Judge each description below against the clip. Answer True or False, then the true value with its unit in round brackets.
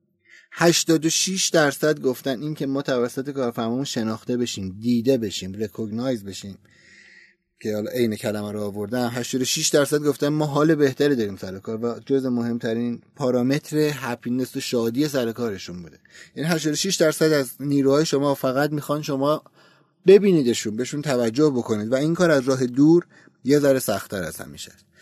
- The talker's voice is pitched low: True (130 Hz)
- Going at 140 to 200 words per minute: True (150 wpm)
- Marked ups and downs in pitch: False (4.2 semitones)